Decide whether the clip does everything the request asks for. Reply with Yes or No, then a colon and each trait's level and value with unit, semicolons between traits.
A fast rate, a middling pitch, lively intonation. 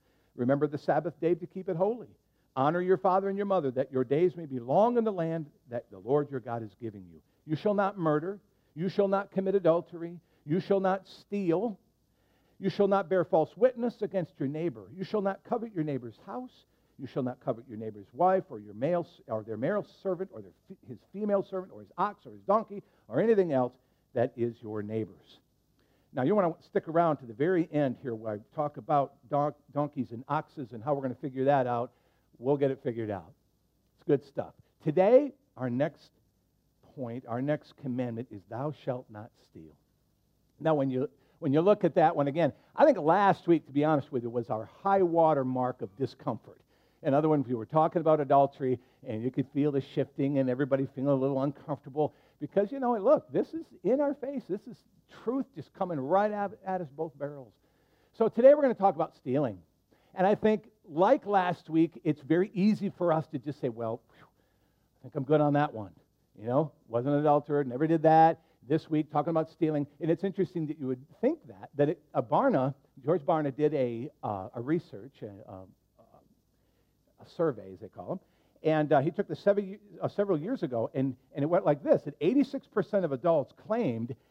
Yes: fast, 210 wpm; medium, 150 Hz; wide, 6.4 semitones